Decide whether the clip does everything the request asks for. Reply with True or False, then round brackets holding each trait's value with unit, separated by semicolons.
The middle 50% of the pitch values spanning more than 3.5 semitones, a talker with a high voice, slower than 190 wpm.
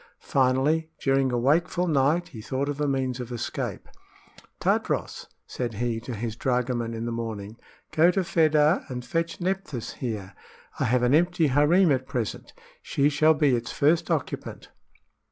False (4.5 semitones; 135 Hz; 160 wpm)